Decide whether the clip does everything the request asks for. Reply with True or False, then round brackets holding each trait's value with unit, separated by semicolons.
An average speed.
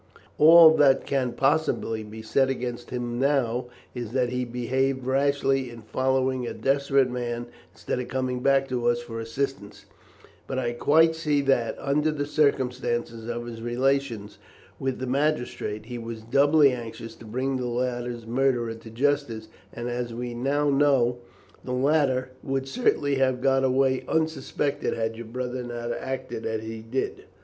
True (160 wpm)